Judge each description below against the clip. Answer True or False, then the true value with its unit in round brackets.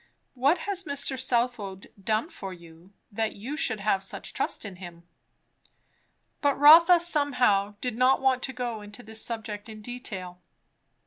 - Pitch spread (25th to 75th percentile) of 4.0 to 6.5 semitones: True (4.9 semitones)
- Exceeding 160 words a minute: False (150 wpm)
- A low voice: False (230 Hz)